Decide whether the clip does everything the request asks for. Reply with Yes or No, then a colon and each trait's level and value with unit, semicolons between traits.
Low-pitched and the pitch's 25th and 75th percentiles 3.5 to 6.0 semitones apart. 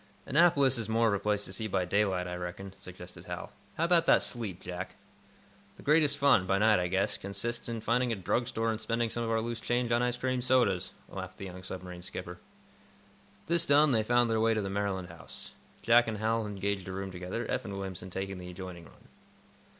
Yes: low, 105 Hz; average, 4.1 semitones